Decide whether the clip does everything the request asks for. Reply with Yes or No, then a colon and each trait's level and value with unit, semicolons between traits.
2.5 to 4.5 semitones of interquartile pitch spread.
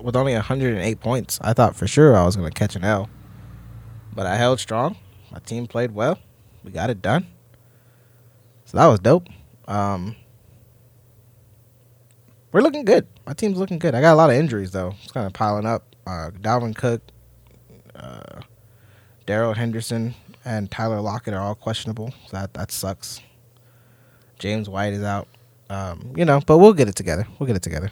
Yes: average, 2.8 semitones